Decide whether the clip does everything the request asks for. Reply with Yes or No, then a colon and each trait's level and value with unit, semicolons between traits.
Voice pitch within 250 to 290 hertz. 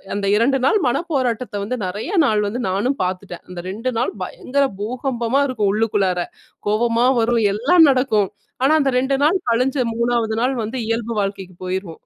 No: high, 230 Hz